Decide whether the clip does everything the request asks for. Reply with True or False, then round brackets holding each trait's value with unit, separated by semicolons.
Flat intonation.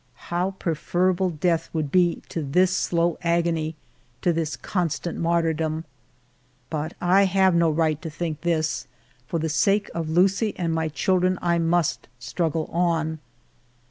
True (1.9 semitones)